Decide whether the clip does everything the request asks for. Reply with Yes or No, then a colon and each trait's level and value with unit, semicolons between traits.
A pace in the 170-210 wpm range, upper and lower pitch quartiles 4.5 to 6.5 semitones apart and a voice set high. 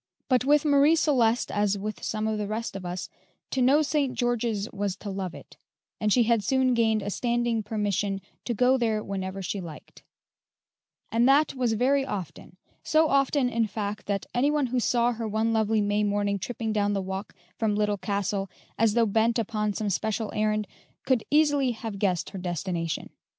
No: average, 190 wpm; average, 3.4 semitones; high, 220 Hz